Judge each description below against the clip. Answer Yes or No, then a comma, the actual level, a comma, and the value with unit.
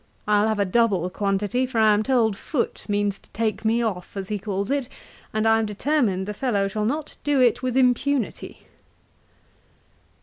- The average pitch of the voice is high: Yes, high, 220 Hz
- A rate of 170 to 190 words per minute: Yes, average, 180 wpm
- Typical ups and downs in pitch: Yes, average, 3.6 semitones